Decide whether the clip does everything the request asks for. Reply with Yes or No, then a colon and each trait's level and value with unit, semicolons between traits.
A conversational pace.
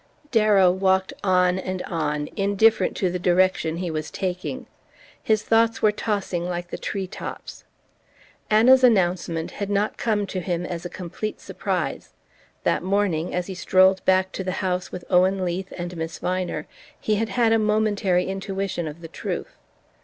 Yes: average, 165 wpm